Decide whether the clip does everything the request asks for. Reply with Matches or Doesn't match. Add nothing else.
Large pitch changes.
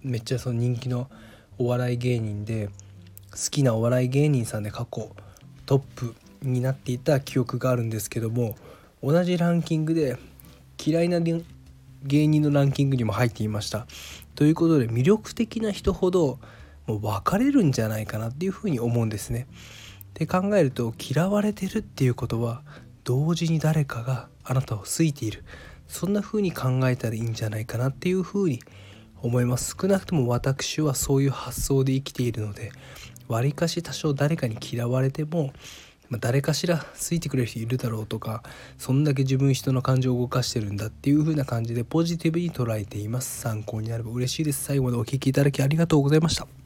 Doesn't match